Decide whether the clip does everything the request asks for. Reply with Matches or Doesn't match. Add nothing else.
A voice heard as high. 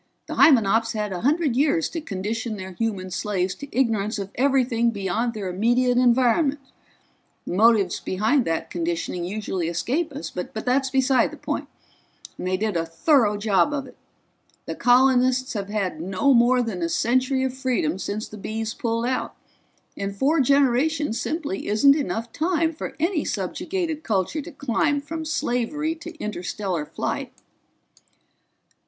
Matches